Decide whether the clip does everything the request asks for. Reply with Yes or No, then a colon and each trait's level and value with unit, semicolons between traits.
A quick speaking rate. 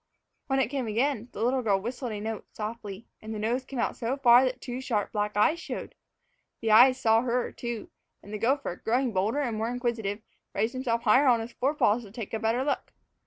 Yes: fast, 220 wpm